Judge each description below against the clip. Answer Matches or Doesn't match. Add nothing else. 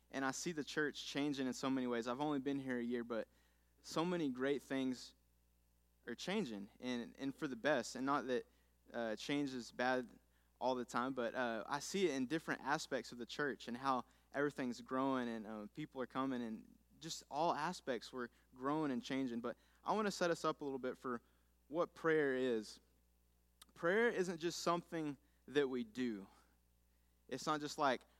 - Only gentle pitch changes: Doesn't match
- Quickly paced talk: Doesn't match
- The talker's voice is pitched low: Matches